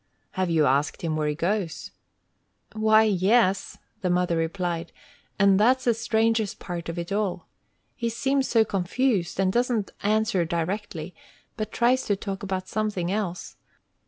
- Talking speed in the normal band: Yes, average, 150 wpm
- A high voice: Yes, high, 195 Hz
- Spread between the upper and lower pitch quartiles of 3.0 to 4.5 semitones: Yes, average, 4.1 semitones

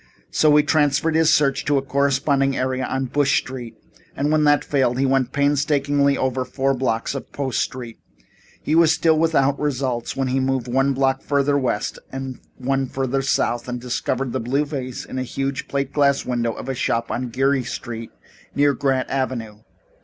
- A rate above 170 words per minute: Yes, average, 185 wpm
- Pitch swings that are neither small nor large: No, narrow, 1.8 semitones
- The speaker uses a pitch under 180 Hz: Yes, low, 135 Hz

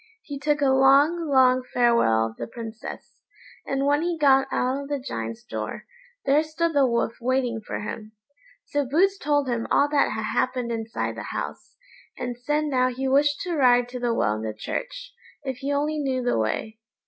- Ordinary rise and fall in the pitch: Yes, average, 3.7 semitones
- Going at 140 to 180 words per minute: No, average, 195 wpm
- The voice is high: Yes, very high, 265 Hz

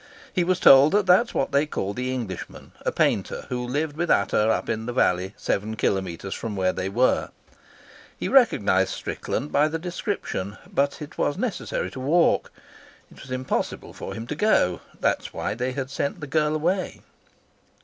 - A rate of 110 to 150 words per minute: No, average, 185 wpm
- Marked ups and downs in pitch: Yes, wide, 6.7 semitones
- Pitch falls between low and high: No, low, 130 Hz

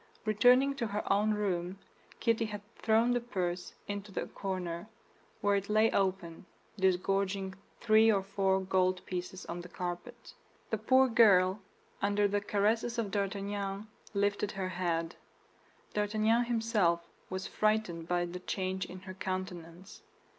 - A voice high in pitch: Yes, high, 195 Hz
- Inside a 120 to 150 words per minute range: Yes, average, 140 wpm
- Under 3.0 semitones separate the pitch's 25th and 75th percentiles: Yes, narrow, 2.6 semitones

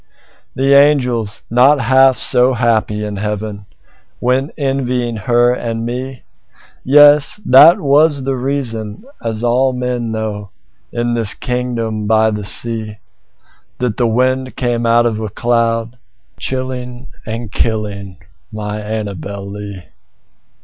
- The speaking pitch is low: Yes, low, 120 Hz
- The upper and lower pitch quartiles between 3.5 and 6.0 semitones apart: No, average, 3.1 semitones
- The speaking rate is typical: No, slow, 115 wpm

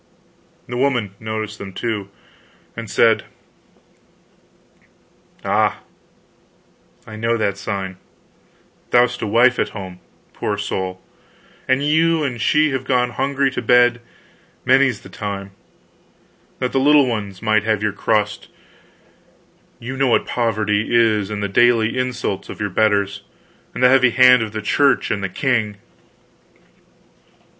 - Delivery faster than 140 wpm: No, slow, 135 wpm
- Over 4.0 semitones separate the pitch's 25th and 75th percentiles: No, average, 3.6 semitones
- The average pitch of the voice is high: No, low, 115 Hz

